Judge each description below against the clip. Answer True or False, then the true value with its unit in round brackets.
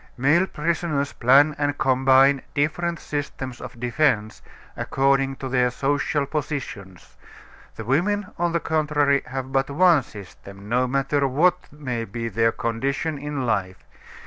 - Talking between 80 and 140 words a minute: True (135 wpm)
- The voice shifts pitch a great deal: False (3.2 semitones)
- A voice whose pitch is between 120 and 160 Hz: True (135 Hz)